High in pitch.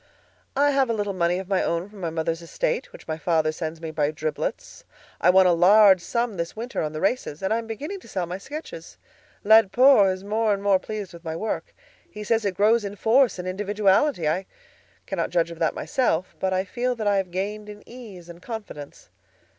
Yes: high, 195 Hz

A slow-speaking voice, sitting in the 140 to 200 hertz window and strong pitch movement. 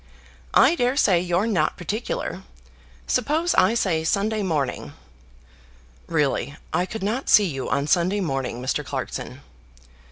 Yes: slow, 125 wpm; medium, 185 Hz; wide, 6.2 semitones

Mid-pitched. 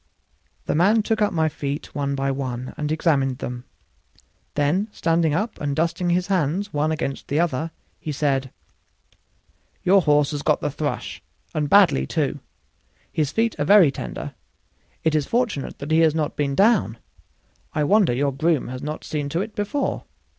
Yes: medium, 155 Hz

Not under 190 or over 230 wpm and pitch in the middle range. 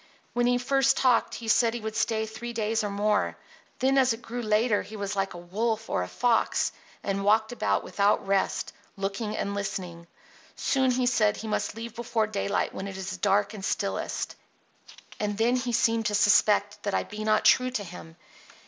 No: average, 195 wpm; high, 215 Hz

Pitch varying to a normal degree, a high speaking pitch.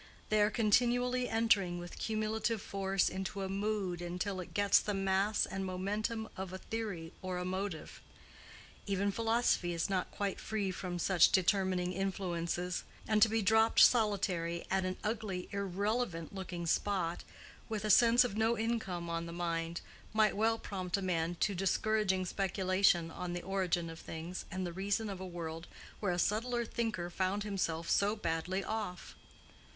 Yes: average, 3.2 semitones; high, 195 Hz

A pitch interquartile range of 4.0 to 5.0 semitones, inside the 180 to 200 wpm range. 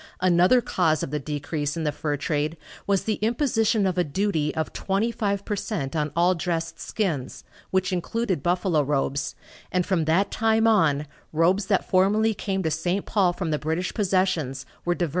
Yes: average, 4.4 semitones; average, 190 wpm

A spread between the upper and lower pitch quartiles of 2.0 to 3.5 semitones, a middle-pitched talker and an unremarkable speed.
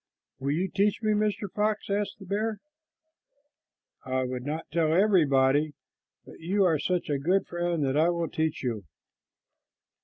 No: wide, 5.5 semitones; medium, 170 Hz; average, 155 wpm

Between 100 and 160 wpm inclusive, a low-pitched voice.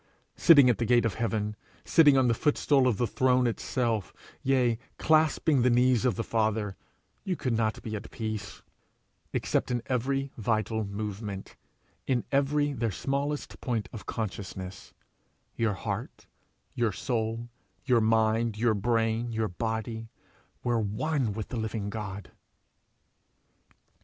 Yes: average, 140 wpm; low, 115 Hz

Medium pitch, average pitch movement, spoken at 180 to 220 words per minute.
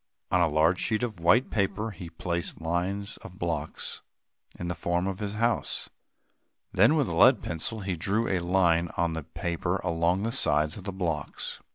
No: very low, 90 Hz; average, 3.2 semitones; average, 185 wpm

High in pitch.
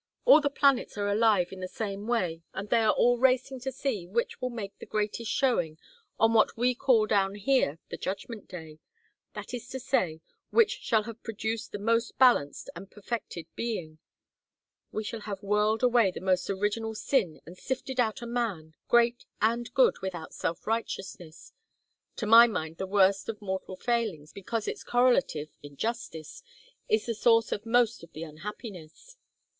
Yes: high, 215 Hz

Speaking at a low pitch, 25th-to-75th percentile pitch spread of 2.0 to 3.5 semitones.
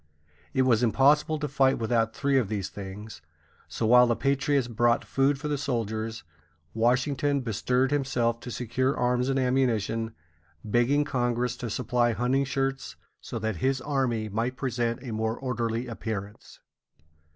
Yes: low, 125 Hz; average, 3.0 semitones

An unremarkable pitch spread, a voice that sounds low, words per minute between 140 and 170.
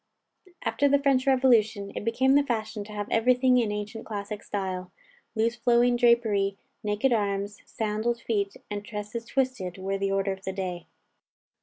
No: average, 3.2 semitones; high, 215 Hz; average, 160 wpm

